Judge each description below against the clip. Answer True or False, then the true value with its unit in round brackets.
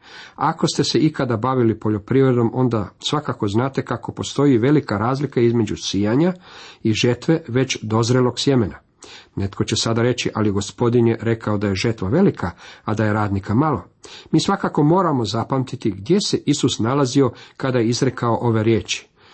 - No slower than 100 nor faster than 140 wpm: False (155 wpm)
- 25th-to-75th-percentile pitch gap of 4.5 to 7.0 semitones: False (3.8 semitones)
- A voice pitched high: False (120 Hz)